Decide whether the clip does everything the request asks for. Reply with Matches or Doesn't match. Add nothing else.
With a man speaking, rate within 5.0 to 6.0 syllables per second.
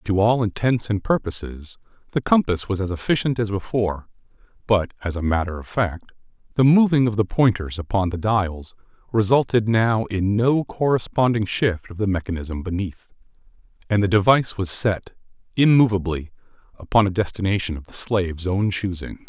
Matches